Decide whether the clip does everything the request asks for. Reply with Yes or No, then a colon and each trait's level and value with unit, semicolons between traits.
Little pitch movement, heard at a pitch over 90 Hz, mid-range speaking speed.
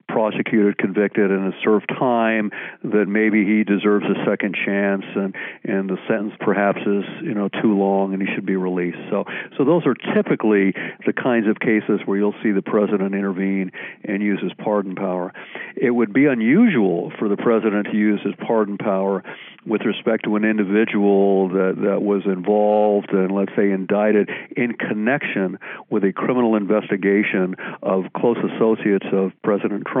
Yes: narrow, 1.8 semitones; low, 105 Hz; average, 170 wpm